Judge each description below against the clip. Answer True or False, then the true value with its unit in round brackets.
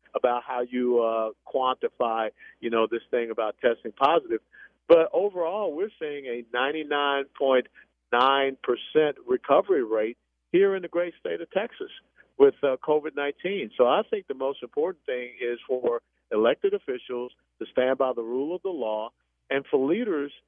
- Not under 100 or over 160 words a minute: True (155 wpm)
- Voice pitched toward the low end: False (145 Hz)